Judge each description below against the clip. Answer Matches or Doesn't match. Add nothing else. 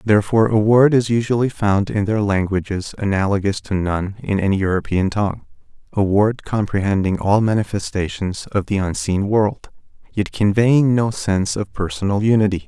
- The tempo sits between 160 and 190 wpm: Doesn't match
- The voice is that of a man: Matches